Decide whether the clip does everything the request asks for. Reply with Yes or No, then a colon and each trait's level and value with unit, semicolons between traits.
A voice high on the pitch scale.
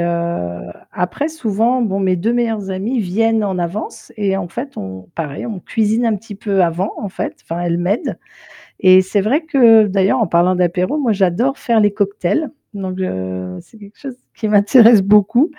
Yes: high, 200 Hz